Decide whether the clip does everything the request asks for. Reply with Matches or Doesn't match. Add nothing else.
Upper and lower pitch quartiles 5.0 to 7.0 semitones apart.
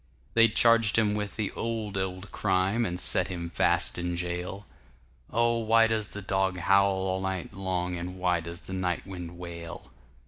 Doesn't match